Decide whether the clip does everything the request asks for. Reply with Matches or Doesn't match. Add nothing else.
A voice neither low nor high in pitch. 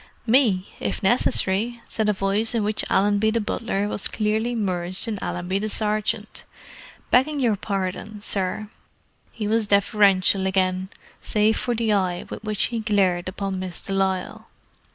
Doesn't match